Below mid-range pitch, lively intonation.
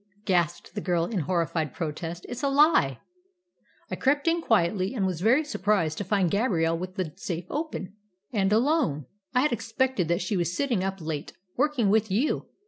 No: high, 195 Hz; wide, 6.3 semitones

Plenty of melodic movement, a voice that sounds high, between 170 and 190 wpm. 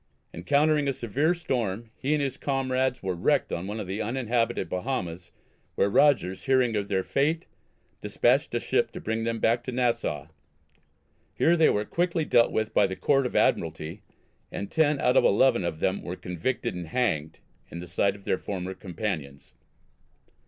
No: wide, 6.0 semitones; low, 115 Hz; average, 175 wpm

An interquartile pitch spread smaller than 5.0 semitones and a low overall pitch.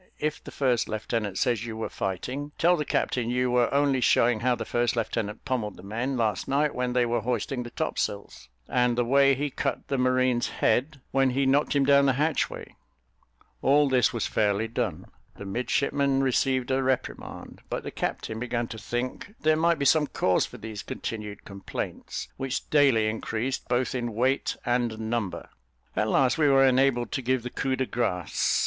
Yes: average, 3.0 semitones; low, 125 Hz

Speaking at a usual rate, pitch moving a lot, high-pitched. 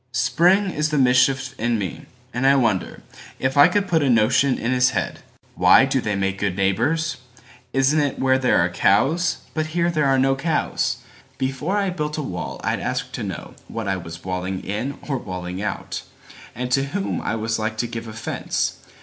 No: average, 175 wpm; wide, 5.9 semitones; low, 130 Hz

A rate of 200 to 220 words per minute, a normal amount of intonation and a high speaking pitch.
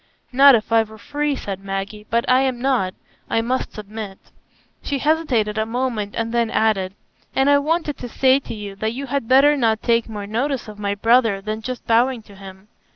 Yes: fast, 205 wpm; average, 3.8 semitones; high, 230 Hz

